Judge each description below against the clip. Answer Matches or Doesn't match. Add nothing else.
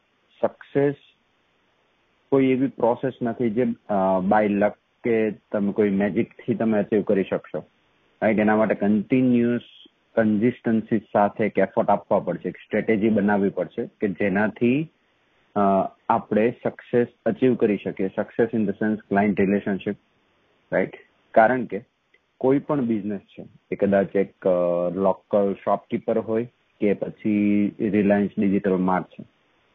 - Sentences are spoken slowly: Matches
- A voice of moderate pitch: Doesn't match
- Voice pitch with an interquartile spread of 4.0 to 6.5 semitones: Doesn't match